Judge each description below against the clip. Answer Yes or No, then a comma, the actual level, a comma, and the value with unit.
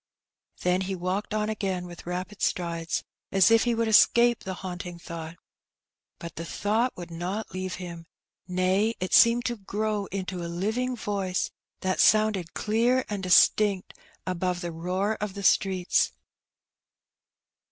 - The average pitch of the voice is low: No, high, 190 Hz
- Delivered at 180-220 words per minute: No, average, 145 wpm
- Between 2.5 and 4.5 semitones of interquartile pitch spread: Yes, average, 3.1 semitones